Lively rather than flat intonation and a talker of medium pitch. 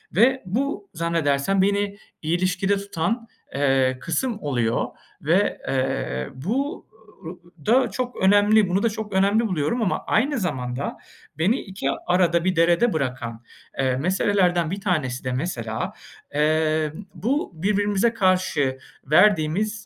Yes: wide, 5.7 semitones; medium, 180 Hz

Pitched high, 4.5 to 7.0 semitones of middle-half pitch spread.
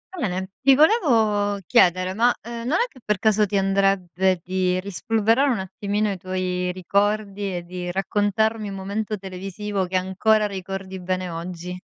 No: high, 195 Hz; narrow, 2.6 semitones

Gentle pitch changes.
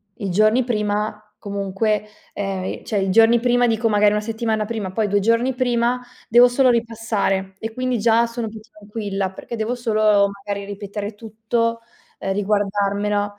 Yes: narrow, 2.2 semitones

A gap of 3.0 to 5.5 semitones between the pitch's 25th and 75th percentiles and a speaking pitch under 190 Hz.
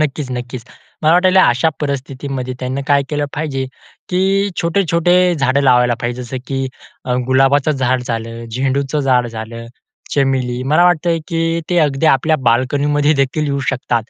Yes: average, 3.6 semitones; medium, 140 Hz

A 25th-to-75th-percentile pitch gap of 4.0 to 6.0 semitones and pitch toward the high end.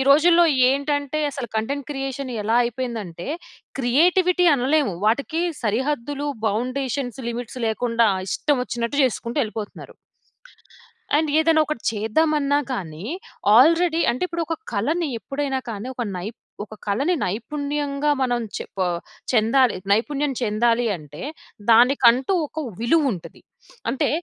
Yes: average, 4.3 semitones; very high, 260 Hz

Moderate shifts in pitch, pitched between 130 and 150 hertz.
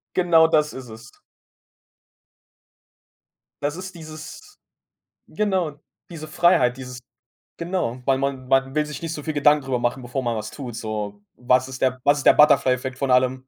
Yes: average, 3.6 semitones; low, 135 Hz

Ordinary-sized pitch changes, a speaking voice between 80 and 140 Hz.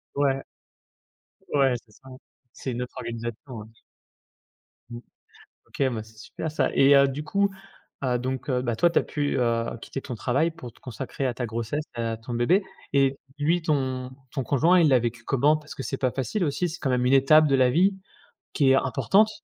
Yes: average, 3.4 semitones; low, 135 Hz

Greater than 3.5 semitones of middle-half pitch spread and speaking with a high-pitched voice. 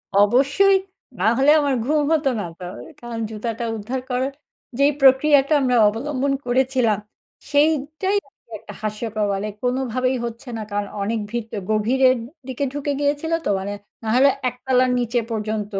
Yes: average, 4.1 semitones; very high, 255 Hz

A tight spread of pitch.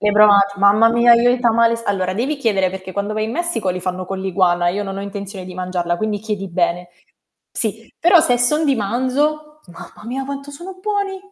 No: average, 5.3 semitones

